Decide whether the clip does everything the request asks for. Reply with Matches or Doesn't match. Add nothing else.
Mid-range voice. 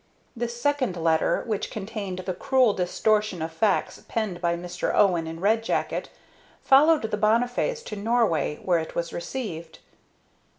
Doesn't match